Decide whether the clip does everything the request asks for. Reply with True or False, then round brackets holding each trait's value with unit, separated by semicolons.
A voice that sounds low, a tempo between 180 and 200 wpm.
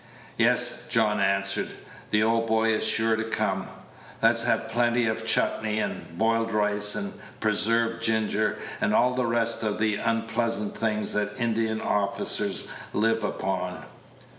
False (110 Hz; 140 wpm)